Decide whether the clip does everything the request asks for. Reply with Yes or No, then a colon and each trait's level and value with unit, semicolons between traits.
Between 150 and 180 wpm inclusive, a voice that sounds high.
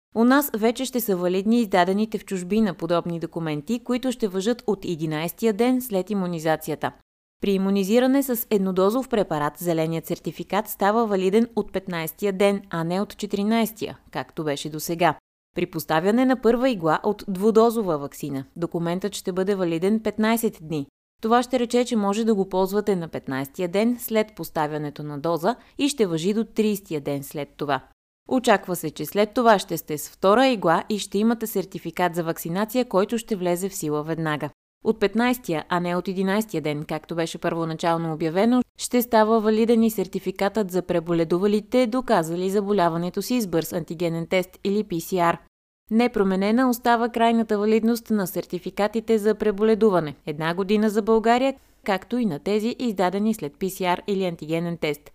Yes: average, 160 wpm; high, 195 Hz